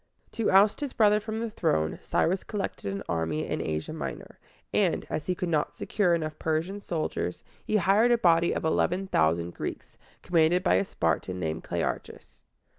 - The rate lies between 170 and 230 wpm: Yes, average, 180 wpm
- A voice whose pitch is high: No, medium, 170 Hz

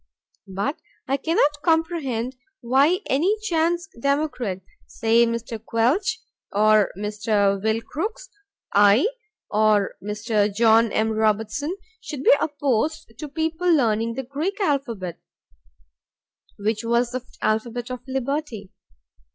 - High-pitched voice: Yes, high, 240 Hz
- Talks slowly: Yes, slow, 110 wpm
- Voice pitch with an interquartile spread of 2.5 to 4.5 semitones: No, wide, 5.6 semitones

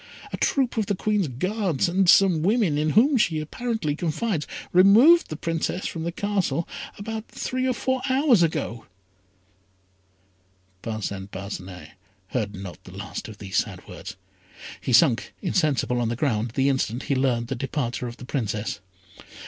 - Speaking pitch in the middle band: Yes, medium, 155 Hz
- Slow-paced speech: No, average, 160 wpm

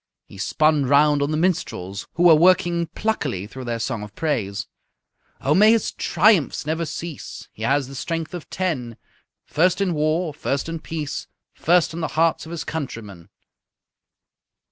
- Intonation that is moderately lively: Yes, average, 4.5 semitones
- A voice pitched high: No, medium, 155 Hz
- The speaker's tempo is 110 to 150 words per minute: No, average, 165 wpm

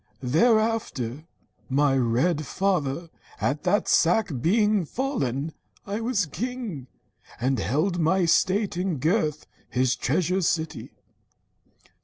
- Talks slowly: Yes, slow, 105 wpm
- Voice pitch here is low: No, medium, 165 Hz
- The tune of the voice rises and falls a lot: Yes, wide, 6.3 semitones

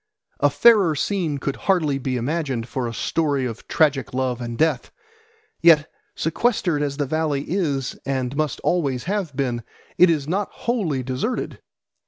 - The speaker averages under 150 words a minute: No, average, 155 wpm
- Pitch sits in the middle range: Yes, medium, 145 Hz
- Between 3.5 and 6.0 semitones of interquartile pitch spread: Yes, average, 4.3 semitones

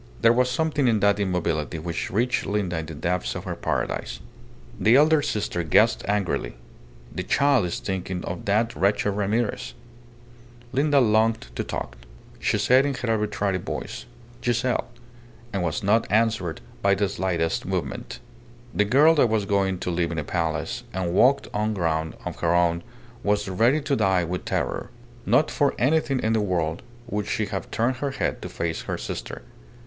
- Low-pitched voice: Yes, low, 100 Hz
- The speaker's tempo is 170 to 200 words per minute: Yes, average, 175 wpm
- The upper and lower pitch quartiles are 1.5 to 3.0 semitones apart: No, average, 5.1 semitones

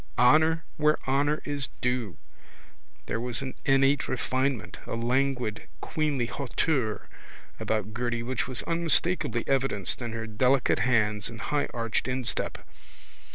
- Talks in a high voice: No, low, 130 Hz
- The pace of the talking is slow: Yes, slow, 120 wpm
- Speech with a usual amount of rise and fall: Yes, average, 3.1 semitones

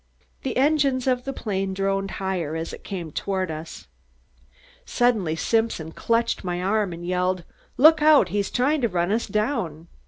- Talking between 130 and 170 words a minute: Yes, average, 160 wpm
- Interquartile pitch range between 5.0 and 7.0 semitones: Yes, wide, 5.6 semitones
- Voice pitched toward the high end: Yes, high, 195 Hz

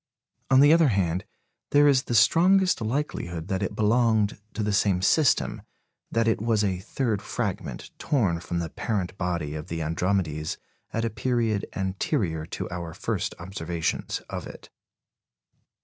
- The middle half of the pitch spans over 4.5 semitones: Yes, average, 5.2 semitones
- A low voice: Yes, low, 100 Hz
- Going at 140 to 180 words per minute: Yes, average, 150 wpm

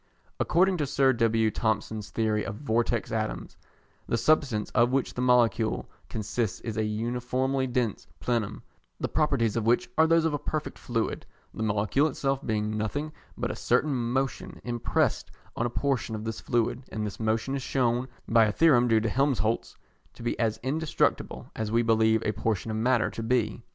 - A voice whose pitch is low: Yes, low, 115 Hz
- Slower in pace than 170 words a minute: No, average, 180 wpm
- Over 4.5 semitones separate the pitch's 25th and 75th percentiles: No, average, 3.2 semitones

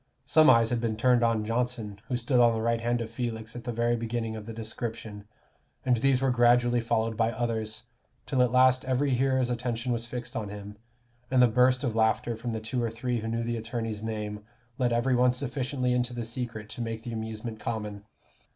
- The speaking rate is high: Yes, fast, 215 wpm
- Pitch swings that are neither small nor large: No, narrow, 1.8 semitones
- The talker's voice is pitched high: No, low, 115 Hz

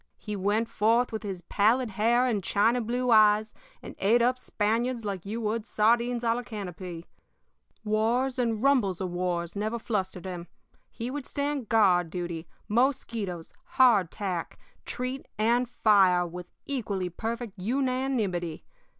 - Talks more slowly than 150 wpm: Yes, average, 140 wpm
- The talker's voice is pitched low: No, high, 215 Hz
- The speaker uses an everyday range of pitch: Yes, average, 4.3 semitones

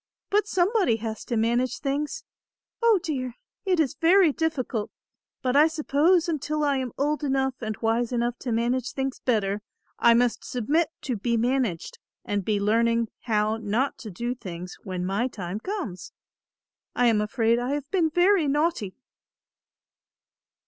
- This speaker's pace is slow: No, average, 155 wpm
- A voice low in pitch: No, very high, 250 Hz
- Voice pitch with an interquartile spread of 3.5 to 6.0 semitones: Yes, average, 5.1 semitones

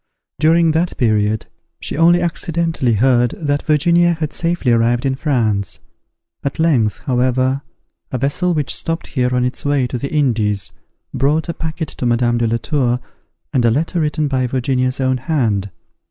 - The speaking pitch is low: Yes, low, 130 Hz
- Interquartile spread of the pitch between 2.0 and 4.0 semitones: No, average, 4.6 semitones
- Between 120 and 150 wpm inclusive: No, average, 165 wpm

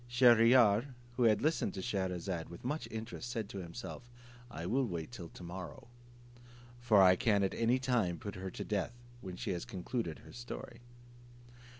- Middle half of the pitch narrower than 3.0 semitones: No, average, 4.8 semitones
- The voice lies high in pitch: No, low, 105 Hz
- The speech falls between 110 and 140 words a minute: No, average, 180 wpm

